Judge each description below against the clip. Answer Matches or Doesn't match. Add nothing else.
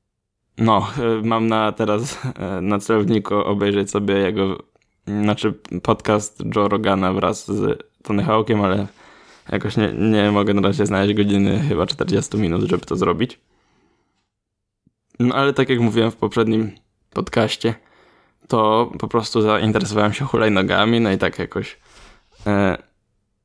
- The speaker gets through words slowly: Doesn't match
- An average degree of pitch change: Doesn't match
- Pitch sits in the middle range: Doesn't match